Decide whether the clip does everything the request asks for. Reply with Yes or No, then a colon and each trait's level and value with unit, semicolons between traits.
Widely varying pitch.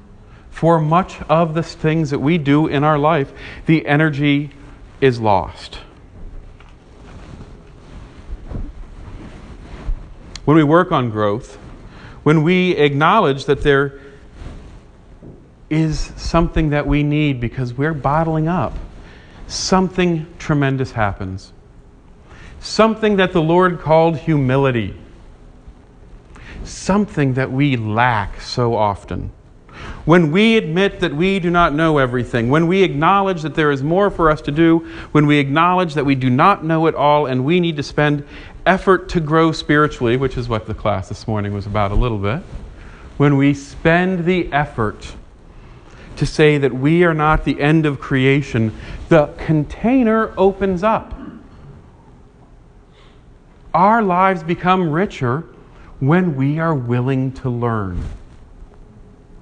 Yes: wide, 6.0 semitones